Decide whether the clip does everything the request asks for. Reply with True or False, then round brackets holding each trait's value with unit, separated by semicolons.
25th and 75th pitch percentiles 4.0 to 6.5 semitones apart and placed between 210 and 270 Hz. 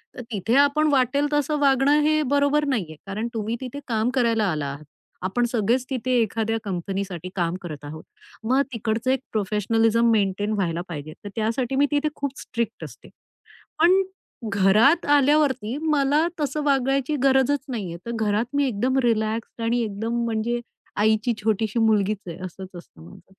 True (4.8 semitones; 230 Hz)